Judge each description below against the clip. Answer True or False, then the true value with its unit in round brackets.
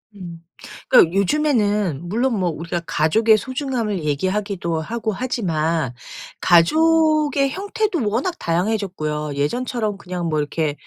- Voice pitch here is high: True (200 Hz)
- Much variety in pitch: True (7.3 semitones)